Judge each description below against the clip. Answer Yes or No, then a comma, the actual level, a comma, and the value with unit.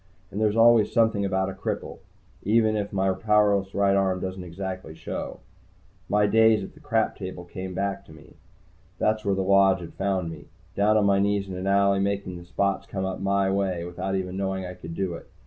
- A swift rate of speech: Yes, fast, 210 wpm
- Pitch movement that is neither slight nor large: No, narrow, 1.5 semitones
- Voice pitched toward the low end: Yes, very low, 95 Hz